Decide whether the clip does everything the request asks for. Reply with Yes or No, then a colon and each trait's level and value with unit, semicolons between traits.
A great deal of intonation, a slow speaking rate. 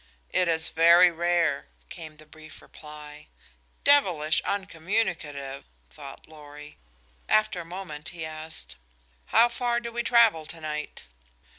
No: average, 3.9 semitones; slow, 120 wpm